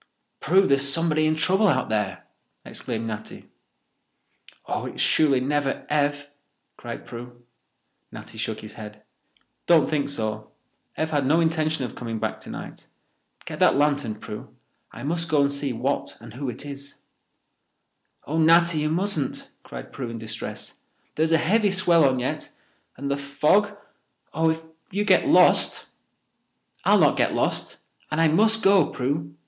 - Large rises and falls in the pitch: No, average, 4.0 semitones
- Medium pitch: Yes, medium, 145 Hz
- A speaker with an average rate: Yes, average, 150 wpm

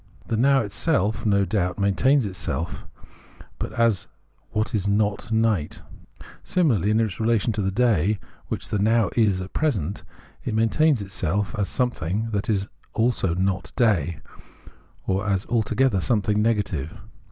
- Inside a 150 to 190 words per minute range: No, average, 140 wpm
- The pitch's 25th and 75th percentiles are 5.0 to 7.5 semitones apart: No, average, 3.0 semitones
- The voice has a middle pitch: No, low, 105 Hz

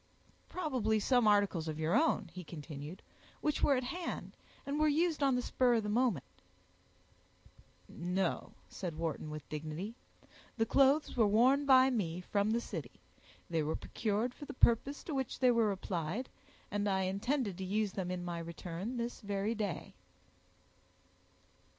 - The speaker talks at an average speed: Yes, average, 160 wpm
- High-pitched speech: Yes, high, 210 Hz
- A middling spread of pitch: No, wide, 6.2 semitones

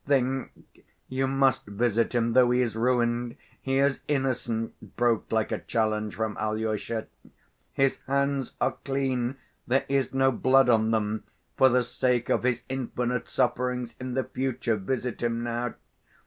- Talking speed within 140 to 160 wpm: Yes, average, 150 wpm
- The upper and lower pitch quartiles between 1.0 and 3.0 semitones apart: Yes, narrow, 2.4 semitones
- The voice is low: Yes, low, 125 Hz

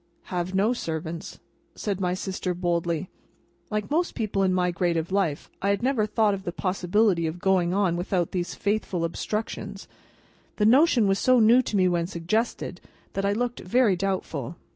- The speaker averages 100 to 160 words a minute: No, average, 175 wpm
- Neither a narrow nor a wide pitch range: Yes, average, 3.4 semitones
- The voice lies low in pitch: No, high, 190 Hz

